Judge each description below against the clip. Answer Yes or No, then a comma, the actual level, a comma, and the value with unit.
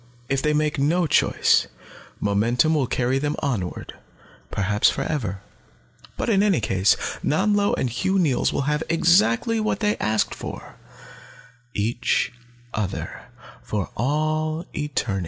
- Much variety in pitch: Yes, wide, 6.1 semitones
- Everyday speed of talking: No, slow, 130 wpm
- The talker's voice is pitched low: No, medium, 145 Hz